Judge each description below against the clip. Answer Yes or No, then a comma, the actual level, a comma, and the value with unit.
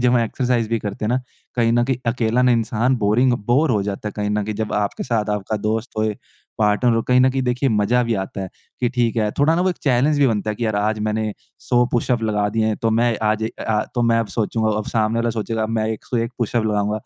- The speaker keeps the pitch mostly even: Yes, narrow, 2.3 semitones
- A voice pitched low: Yes, low, 115 Hz